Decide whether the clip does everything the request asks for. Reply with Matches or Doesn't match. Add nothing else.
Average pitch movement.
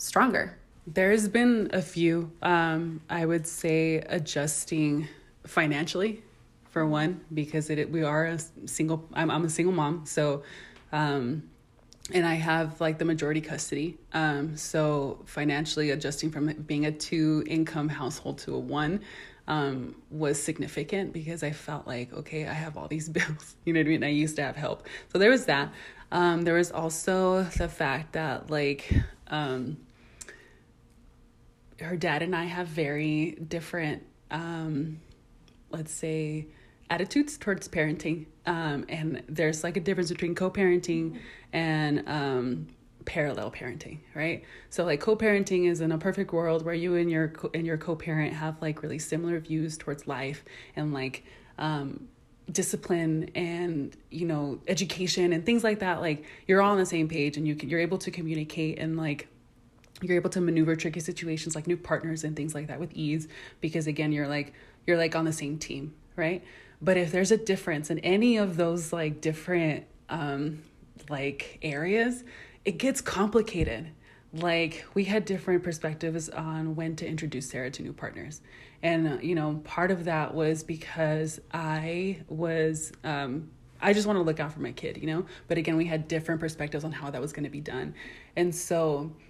Doesn't match